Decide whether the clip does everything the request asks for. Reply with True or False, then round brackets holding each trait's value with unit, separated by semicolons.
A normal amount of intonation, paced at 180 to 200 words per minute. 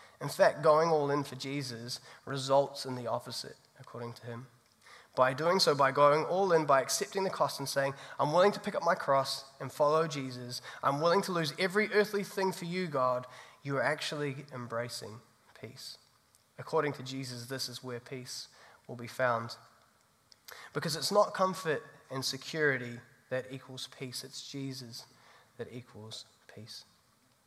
False (3.9 semitones; 165 wpm)